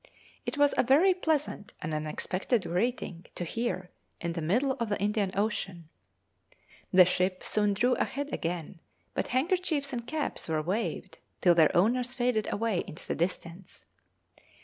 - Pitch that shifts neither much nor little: No, wide, 6.2 semitones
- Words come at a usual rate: Yes, average, 150 wpm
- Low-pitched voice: No, high, 205 Hz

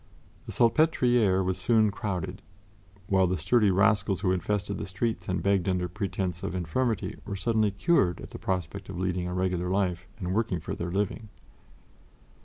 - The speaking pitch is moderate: No, very low, 95 Hz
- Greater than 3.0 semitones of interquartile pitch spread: No, narrow, 2.6 semitones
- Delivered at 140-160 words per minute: No, average, 170 wpm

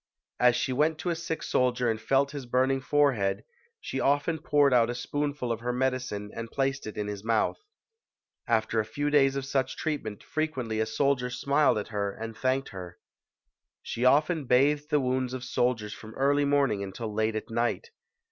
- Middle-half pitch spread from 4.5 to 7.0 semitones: No, average, 4.0 semitones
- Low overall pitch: Yes, low, 125 Hz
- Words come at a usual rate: Yes, average, 185 wpm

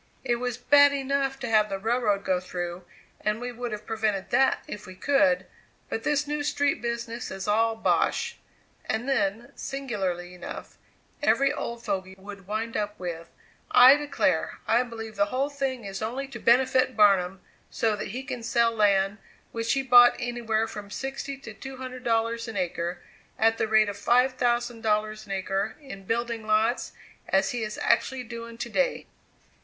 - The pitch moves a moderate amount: Yes, average, 3.6 semitones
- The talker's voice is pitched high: Yes, high, 230 Hz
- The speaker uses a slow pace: No, average, 175 wpm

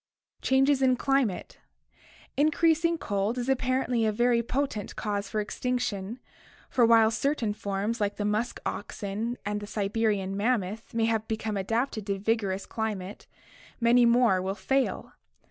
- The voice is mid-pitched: No, high, 225 Hz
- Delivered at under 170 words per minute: Yes, average, 145 wpm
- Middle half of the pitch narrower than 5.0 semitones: Yes, average, 3.4 semitones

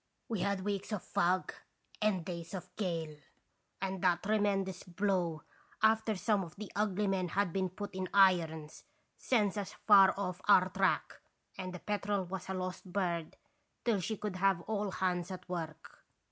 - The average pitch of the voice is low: No, high, 190 Hz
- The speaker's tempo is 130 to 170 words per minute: Yes, average, 165 wpm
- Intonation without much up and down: Yes, narrow, 2.2 semitones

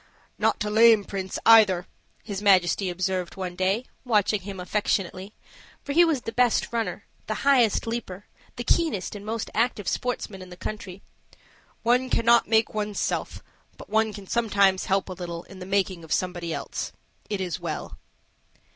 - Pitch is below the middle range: No, high, 205 Hz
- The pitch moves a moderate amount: Yes, average, 3.4 semitones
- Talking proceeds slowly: No, average, 165 wpm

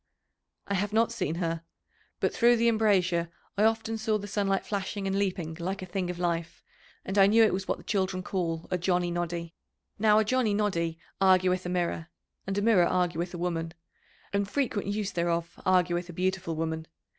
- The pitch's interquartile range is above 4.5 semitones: No, average, 3.0 semitones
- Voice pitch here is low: No, medium, 185 Hz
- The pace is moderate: Yes, average, 190 wpm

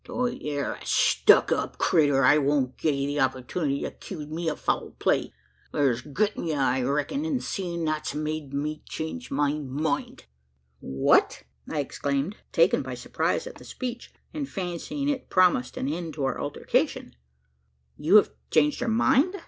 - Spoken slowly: No, average, 175 wpm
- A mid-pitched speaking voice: Yes, medium, 150 Hz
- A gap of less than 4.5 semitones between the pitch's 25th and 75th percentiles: No, average, 4.9 semitones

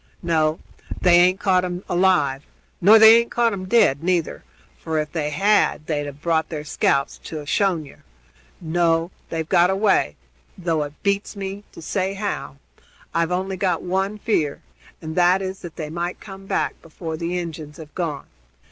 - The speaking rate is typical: Yes, average, 175 wpm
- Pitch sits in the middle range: Yes, medium, 175 Hz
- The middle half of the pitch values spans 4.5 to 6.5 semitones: No, average, 3.5 semitones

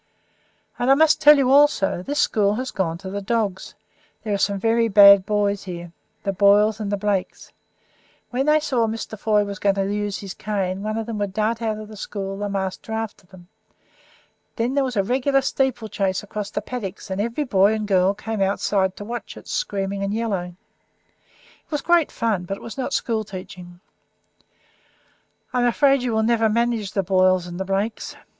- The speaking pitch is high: Yes, high, 210 Hz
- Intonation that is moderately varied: Yes, average, 3.0 semitones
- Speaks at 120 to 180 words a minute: No, average, 195 wpm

